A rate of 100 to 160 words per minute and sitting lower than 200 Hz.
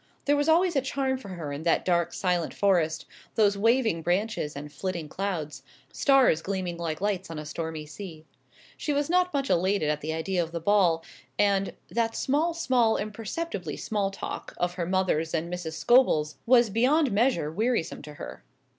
No: average, 180 wpm; high, 190 Hz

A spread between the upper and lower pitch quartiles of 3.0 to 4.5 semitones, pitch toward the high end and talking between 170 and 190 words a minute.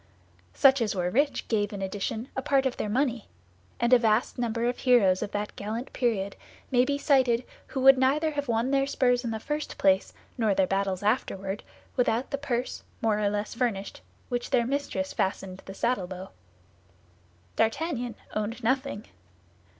Yes: average, 4.2 semitones; high, 235 Hz; average, 175 wpm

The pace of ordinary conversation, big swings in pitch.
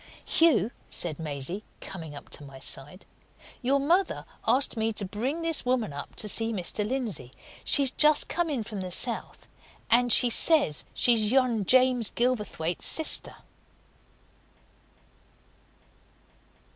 No: slow, 130 wpm; wide, 6.3 semitones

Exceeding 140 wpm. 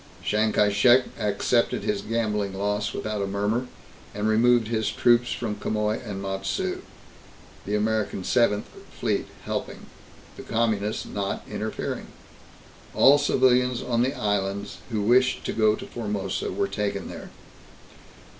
No: slow, 135 wpm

